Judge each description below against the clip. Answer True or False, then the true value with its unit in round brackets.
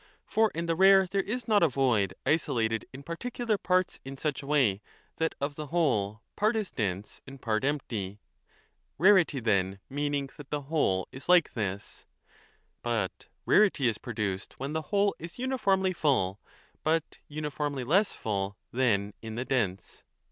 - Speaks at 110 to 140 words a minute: False (165 wpm)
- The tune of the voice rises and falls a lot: True (7.7 semitones)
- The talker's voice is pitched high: False (140 Hz)